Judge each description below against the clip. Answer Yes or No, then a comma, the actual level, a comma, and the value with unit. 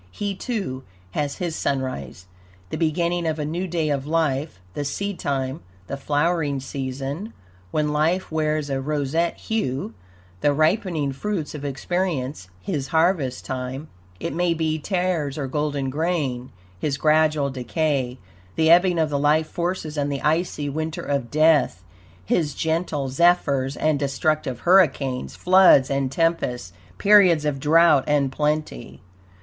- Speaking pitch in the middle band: Yes, medium, 150 Hz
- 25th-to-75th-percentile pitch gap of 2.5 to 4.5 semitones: Yes, average, 3.4 semitones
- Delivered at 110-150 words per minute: Yes, average, 140 wpm